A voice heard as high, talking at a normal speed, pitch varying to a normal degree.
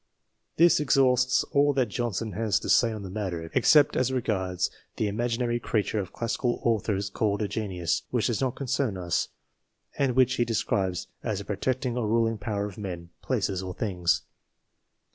No: low, 110 Hz; average, 170 wpm; average, 3.9 semitones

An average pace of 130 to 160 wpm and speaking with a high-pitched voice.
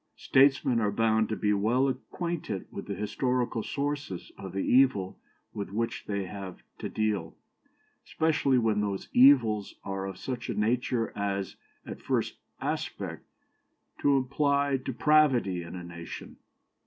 No: average, 140 wpm; low, 115 Hz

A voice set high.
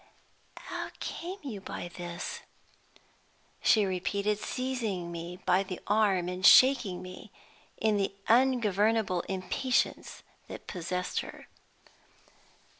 Yes: high, 195 Hz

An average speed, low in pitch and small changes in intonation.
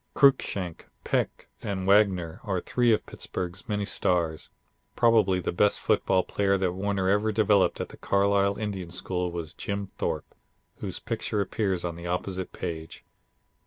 Yes: average, 150 wpm; very low, 95 Hz; narrow, 2.3 semitones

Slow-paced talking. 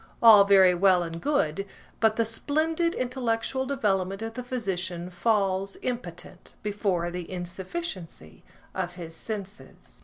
Yes: slow, 125 wpm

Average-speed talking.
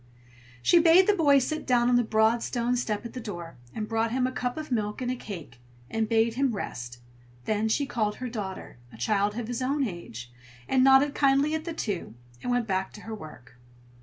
No: fast, 220 wpm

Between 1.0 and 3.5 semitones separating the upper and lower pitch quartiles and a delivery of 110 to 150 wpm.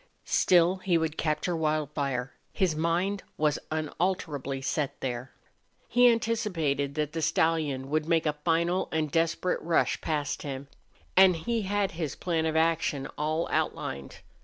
Yes: average, 2.9 semitones; average, 140 wpm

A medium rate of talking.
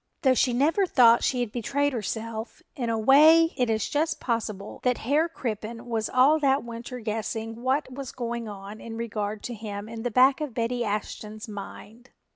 Yes: average, 185 wpm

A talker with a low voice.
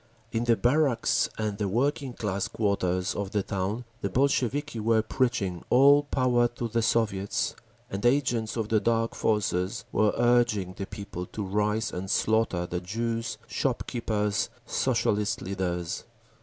Yes: low, 110 Hz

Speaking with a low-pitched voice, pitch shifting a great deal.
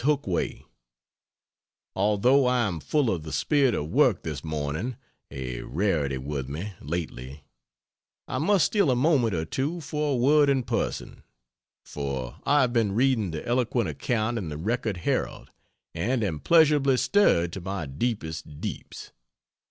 Yes: low, 105 Hz; wide, 8.9 semitones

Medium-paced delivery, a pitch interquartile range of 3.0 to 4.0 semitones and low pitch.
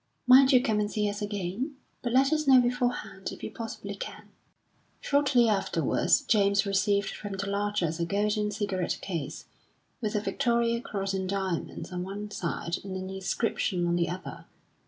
No: average, 170 wpm; average, 3.4 semitones; high, 205 Hz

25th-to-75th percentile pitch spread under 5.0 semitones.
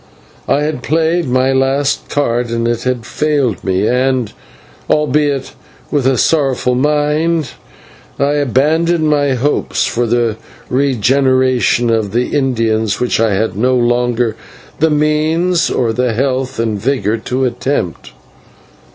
Yes: average, 3.7 semitones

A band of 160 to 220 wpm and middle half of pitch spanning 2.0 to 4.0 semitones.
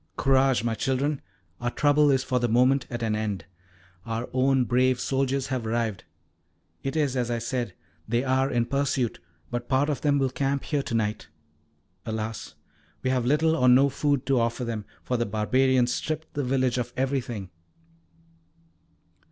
Yes: average, 170 wpm; narrow, 2.5 semitones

